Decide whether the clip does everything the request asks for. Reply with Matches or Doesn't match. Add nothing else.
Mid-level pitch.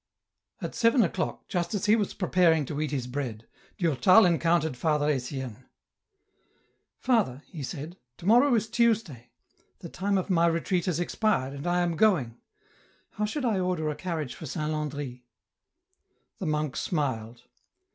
Matches